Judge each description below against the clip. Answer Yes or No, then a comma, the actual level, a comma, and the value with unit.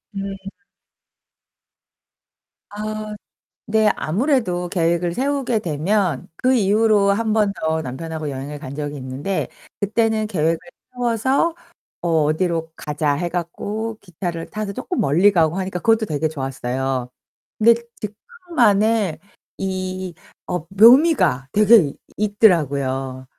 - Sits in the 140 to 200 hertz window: Yes, high, 190 Hz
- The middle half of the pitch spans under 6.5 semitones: Yes, wide, 5.6 semitones